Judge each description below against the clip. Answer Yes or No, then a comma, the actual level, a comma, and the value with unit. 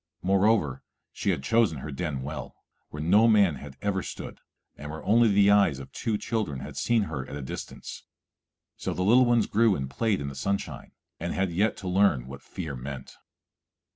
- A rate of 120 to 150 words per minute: No, average, 195 wpm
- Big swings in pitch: Yes, wide, 6.8 semitones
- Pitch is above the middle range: No, very low, 90 Hz